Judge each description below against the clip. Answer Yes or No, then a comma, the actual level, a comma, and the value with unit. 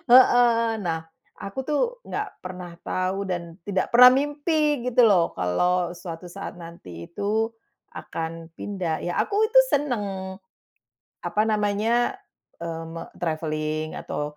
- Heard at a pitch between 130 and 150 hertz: No, high, 190 Hz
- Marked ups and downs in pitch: Yes, wide, 6.0 semitones